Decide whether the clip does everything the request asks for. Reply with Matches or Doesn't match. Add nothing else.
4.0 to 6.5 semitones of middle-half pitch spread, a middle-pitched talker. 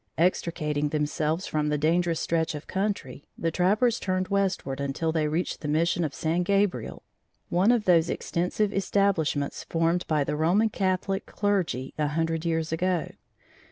Doesn't match